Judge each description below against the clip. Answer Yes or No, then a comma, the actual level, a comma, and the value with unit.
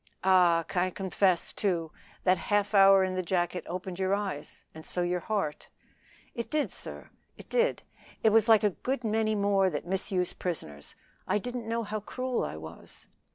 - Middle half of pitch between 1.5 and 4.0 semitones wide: Yes, average, 3.3 semitones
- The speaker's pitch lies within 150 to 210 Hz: Yes, high, 190 Hz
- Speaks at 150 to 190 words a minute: Yes, average, 170 wpm